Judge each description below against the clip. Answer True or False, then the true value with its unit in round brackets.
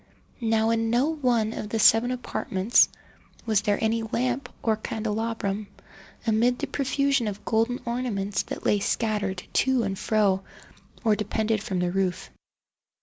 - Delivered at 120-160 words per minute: True (145 wpm)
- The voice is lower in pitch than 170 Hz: False (220 Hz)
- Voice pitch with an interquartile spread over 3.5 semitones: False (2.6 semitones)